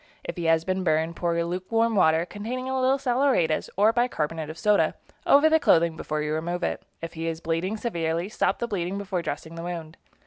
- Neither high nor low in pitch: Yes, medium, 175 Hz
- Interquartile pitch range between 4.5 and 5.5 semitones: Yes, average, 5.2 semitones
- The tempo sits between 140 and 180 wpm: No, fast, 205 wpm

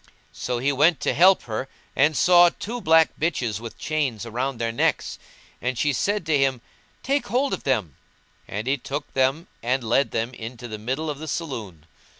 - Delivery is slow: No, average, 185 wpm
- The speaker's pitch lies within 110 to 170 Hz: Yes, low, 135 Hz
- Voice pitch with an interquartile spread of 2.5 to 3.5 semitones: No, average, 5.2 semitones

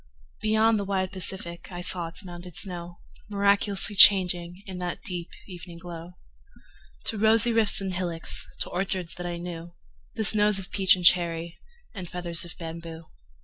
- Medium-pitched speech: Yes, medium, 180 Hz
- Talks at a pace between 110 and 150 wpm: No, average, 160 wpm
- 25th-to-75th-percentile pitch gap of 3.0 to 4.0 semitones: No, narrow, 2.5 semitones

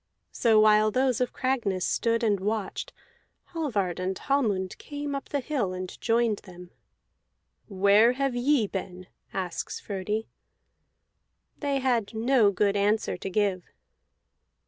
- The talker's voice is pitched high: Yes, high, 215 Hz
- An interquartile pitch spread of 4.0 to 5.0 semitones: Yes, average, 4.5 semitones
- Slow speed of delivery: Yes, slow, 125 wpm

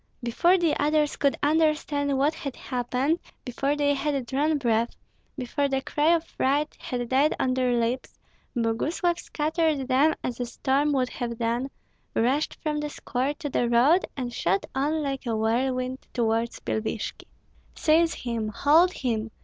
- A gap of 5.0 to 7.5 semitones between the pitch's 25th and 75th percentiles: No, average, 3.6 semitones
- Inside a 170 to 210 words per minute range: No, average, 155 wpm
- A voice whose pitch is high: Yes, very high, 270 Hz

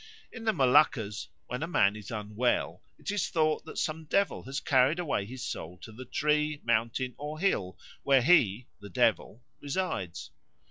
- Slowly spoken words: No, average, 170 wpm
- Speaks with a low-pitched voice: Yes, low, 130 Hz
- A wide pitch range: Yes, wide, 6.0 semitones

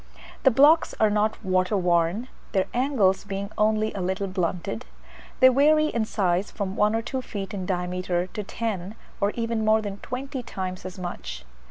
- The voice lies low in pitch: No, high, 205 Hz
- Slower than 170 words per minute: No, average, 175 wpm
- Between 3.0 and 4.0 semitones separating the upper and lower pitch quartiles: Yes, average, 3.6 semitones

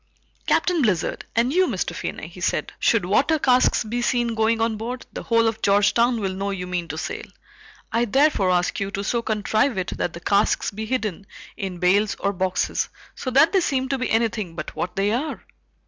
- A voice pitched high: Yes, high, 220 Hz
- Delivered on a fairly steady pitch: No, average, 3.9 semitones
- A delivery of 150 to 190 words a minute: No, fast, 205 wpm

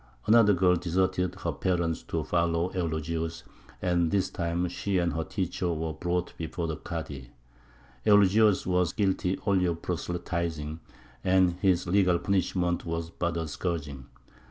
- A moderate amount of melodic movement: No, narrow, 1.9 semitones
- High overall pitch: No, very low, 85 Hz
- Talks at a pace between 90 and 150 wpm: Yes, average, 140 wpm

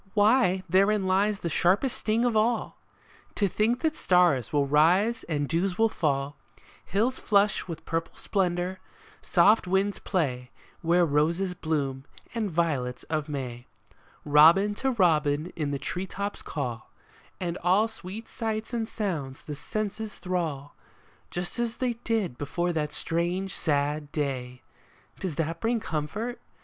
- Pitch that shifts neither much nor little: No, wide, 5.8 semitones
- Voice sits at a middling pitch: Yes, medium, 180 Hz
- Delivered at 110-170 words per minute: Yes, average, 140 wpm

